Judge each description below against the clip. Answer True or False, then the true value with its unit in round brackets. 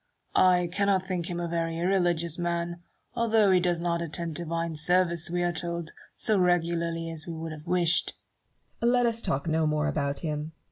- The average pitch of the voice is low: False (170 Hz)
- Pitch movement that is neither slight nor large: False (1.5 semitones)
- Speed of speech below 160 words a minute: False (185 wpm)